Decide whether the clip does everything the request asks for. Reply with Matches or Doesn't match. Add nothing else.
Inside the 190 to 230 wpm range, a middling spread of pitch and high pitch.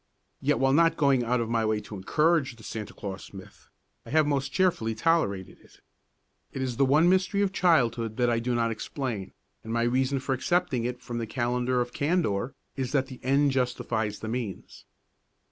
Doesn't match